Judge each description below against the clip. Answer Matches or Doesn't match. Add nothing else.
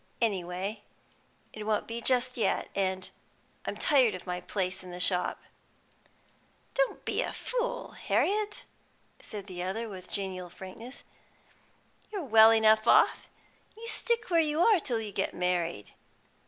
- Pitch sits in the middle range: Doesn't match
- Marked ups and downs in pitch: Matches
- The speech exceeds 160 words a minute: Doesn't match